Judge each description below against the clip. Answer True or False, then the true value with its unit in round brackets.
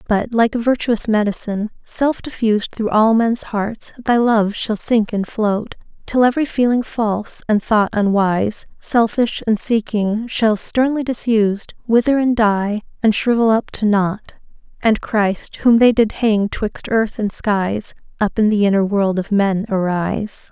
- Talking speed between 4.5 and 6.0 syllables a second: False (4.2 syllables/s)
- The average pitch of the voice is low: False (215 Hz)